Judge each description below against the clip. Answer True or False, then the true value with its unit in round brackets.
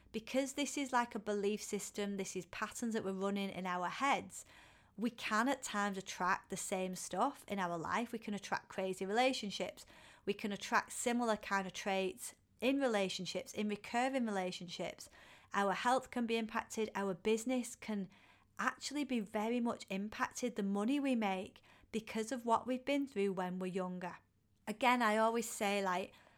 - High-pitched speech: True (210 Hz)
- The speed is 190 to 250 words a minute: False (170 wpm)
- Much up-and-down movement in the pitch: False (3.8 semitones)